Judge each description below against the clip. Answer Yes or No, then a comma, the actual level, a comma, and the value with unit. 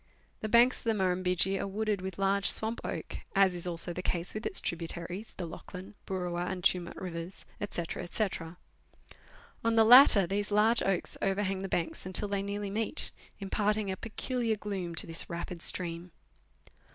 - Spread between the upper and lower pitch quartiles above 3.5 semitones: No, average, 2.8 semitones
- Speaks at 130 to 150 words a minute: No, average, 175 wpm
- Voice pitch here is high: Yes, high, 195 Hz